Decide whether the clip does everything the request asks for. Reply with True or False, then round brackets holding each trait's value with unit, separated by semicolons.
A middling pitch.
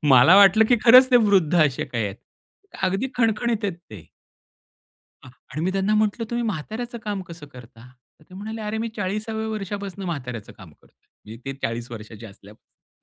False (195 Hz)